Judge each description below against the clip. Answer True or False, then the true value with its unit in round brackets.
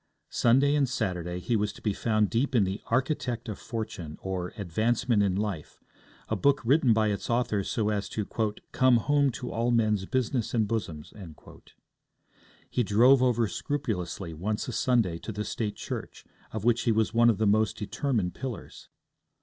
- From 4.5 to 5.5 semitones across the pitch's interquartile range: False (3.2 semitones)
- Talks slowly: False (175 wpm)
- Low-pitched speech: True (110 Hz)